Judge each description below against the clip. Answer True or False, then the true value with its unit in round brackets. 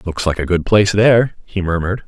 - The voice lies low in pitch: True (95 Hz)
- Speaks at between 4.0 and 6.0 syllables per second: False (6.5 syllables/s)